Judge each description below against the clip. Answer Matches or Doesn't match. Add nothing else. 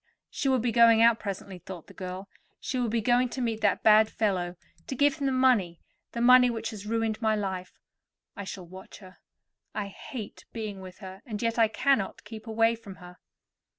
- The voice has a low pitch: Doesn't match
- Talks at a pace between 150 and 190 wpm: Doesn't match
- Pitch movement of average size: Matches